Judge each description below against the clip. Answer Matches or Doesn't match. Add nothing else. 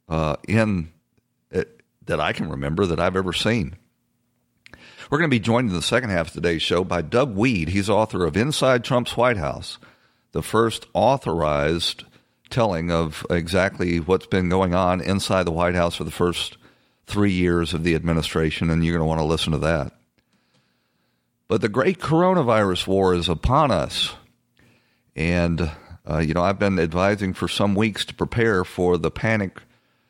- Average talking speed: Matches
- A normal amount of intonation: Matches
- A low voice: Matches